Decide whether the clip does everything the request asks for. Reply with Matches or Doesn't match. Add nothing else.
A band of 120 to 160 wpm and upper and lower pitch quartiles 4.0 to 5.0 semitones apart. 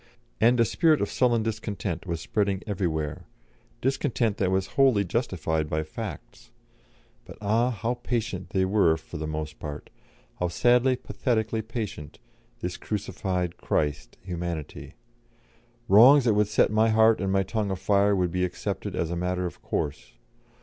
Matches